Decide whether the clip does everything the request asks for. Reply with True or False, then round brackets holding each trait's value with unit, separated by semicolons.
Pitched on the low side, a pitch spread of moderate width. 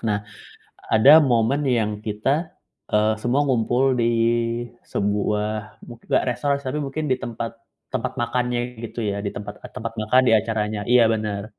True (115 Hz; 3.1 semitones)